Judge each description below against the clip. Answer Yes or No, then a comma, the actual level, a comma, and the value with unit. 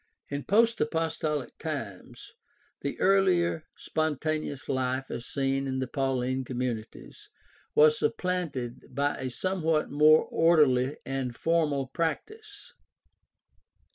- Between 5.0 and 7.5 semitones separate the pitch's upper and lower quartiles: No, average, 3.8 semitones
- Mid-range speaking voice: Yes, medium, 145 Hz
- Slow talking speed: Yes, slow, 110 wpm